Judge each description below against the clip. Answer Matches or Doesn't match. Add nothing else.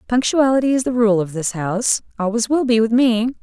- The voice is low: Doesn't match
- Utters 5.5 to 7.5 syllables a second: Matches